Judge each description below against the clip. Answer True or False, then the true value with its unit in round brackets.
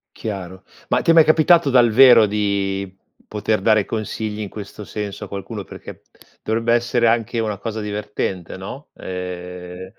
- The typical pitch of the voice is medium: False (105 Hz)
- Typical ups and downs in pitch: True (3.1 semitones)